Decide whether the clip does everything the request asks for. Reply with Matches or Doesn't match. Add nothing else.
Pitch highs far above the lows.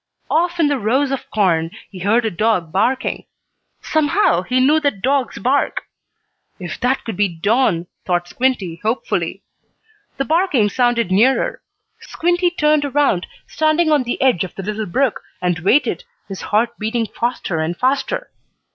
Matches